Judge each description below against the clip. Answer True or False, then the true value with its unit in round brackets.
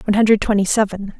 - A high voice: True (205 Hz)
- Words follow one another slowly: False (200 wpm)